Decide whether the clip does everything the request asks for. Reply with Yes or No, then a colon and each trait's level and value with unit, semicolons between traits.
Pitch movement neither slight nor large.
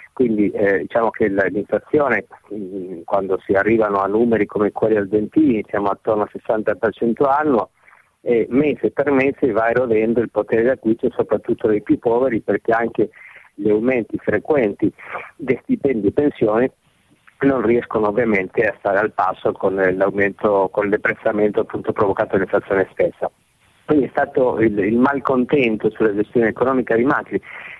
Yes: average, 3.6 semitones